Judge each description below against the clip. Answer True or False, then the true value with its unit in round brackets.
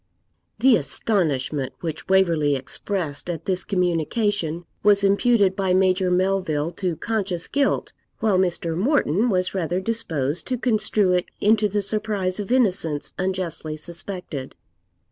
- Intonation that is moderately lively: True (3.7 semitones)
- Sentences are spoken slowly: True (125 wpm)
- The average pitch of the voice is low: False (185 Hz)